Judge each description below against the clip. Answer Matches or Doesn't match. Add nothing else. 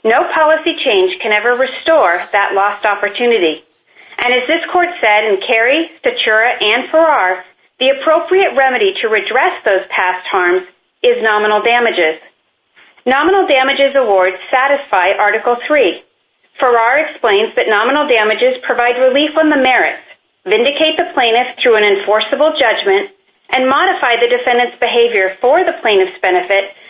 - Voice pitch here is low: Doesn't match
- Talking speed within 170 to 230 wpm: Doesn't match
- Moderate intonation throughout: Doesn't match